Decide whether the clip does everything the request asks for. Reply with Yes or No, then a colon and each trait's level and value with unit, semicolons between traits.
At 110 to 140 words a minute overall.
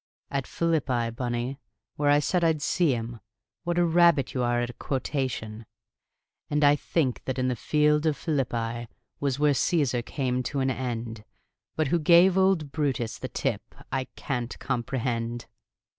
No: average, 160 wpm